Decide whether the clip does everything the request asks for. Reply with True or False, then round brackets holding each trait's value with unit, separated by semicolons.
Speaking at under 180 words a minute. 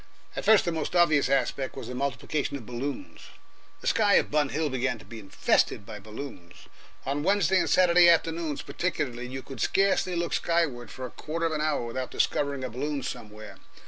False (190 wpm)